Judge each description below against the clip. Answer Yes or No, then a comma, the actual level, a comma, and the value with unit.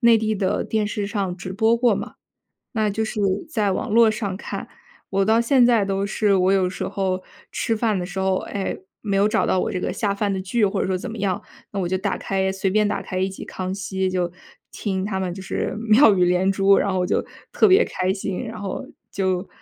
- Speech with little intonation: Yes, narrow, 2.3 semitones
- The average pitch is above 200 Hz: No, high, 195 Hz